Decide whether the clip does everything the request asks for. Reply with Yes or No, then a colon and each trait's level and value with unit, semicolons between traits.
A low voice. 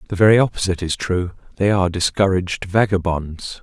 Yes: very low, 95 Hz